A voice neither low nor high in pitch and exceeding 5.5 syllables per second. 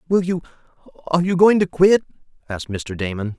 Yes: medium, 155 Hz; 6.3 syllables/s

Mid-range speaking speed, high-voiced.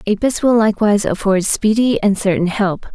Yes: average, 165 wpm; high, 210 Hz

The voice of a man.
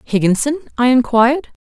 No: female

